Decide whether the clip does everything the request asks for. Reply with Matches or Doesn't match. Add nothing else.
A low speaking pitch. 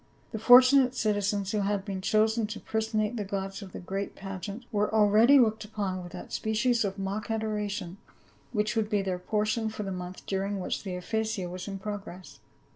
Doesn't match